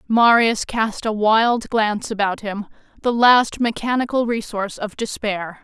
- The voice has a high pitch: Yes, high, 220 Hz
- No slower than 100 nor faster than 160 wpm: Yes, average, 140 wpm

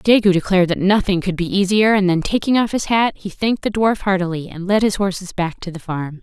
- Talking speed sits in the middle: No, fast, 250 wpm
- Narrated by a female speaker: Yes, female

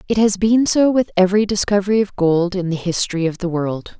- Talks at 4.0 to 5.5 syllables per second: No, 5.9 syllables/s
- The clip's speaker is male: No, female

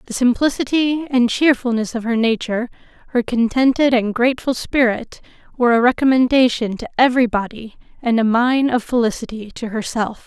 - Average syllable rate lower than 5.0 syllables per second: No, 5.6 syllables/s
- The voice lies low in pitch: No, high, 240 Hz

